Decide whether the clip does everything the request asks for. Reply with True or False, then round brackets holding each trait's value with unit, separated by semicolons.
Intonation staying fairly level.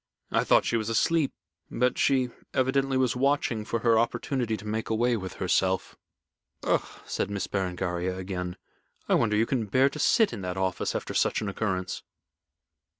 False (5.2 semitones)